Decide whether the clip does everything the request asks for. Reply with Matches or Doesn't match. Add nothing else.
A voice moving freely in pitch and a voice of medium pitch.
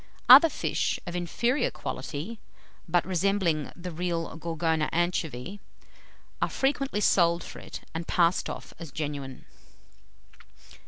Doesn't match